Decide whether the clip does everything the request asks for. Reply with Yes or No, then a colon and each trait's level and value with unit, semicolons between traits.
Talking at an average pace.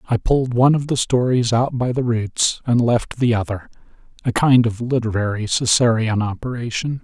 Yes: average, 160 wpm